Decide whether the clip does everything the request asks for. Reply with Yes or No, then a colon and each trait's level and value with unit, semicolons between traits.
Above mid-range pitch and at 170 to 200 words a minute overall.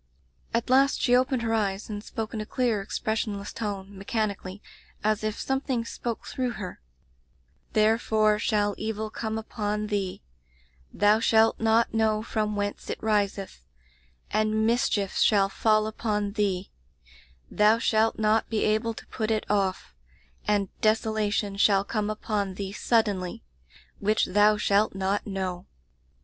No: high, 215 Hz; average, 140 wpm